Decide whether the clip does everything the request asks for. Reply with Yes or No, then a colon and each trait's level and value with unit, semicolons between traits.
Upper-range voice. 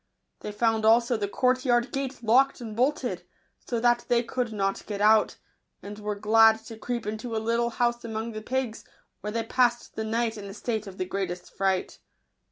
Yes: high, 225 Hz